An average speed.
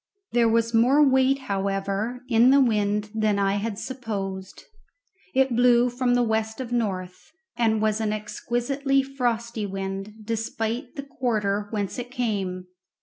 Yes: average, 145 wpm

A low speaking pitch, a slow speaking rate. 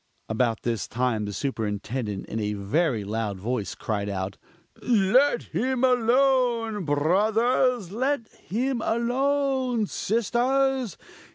No: high, 210 Hz; slow, 105 wpm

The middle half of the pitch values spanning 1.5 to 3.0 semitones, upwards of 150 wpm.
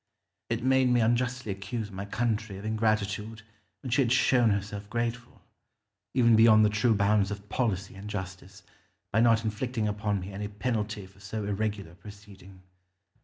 Yes: narrow, 2.5 semitones; average, 165 wpm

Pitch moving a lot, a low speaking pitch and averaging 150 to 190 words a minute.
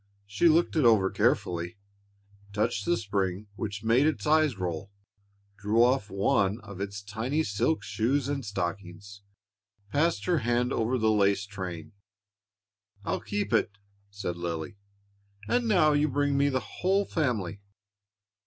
No: wide, 6.1 semitones; low, 110 Hz; average, 140 wpm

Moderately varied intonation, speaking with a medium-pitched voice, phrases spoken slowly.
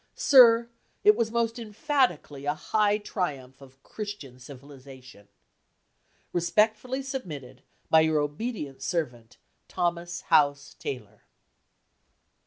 No: wide, 8.2 semitones; medium, 165 Hz; slow, 95 wpm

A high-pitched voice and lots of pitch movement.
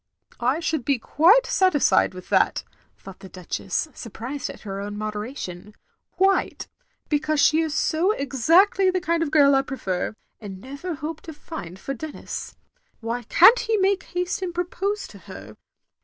Yes: very high, 290 Hz; wide, 8.1 semitones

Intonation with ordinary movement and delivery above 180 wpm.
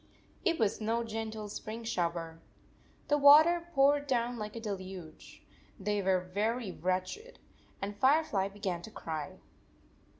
No: average, 5.0 semitones; slow, 135 wpm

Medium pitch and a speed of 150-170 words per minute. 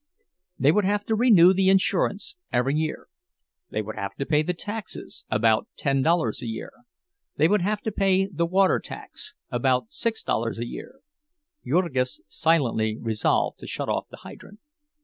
Yes: medium, 170 Hz; average, 165 wpm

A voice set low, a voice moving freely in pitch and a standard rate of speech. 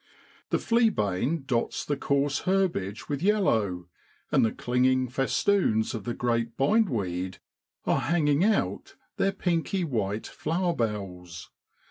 No: low, 130 Hz; wide, 8.4 semitones; slow, 125 wpm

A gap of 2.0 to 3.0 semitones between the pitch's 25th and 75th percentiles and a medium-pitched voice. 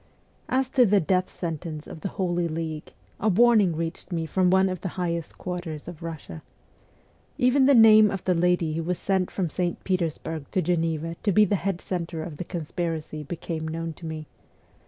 Yes: average, 2.7 semitones; medium, 175 Hz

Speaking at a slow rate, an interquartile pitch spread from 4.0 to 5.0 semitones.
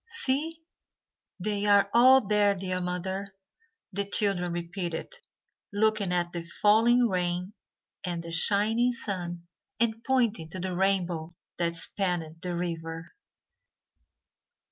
No: slow, 115 wpm; average, 3.5 semitones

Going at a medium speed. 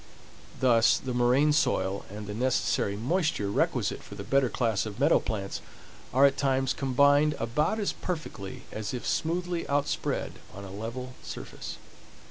Yes: average, 150 wpm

